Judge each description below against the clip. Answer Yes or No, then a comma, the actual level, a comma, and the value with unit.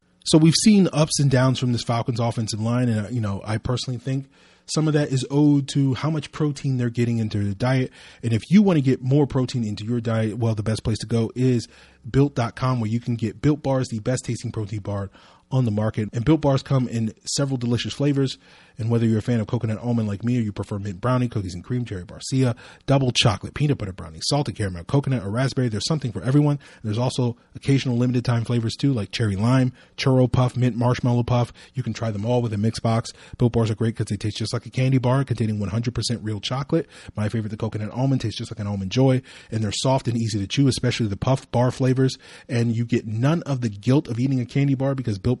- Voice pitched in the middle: No, low, 120 Hz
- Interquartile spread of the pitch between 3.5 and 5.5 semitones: No, average, 3.0 semitones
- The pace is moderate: No, fast, 245 wpm